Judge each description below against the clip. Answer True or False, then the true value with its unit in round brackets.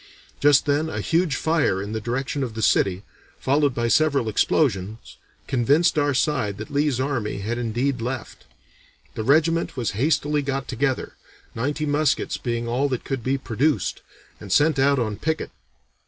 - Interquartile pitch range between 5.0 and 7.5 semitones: False (4.0 semitones)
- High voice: False (135 Hz)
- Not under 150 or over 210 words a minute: True (160 wpm)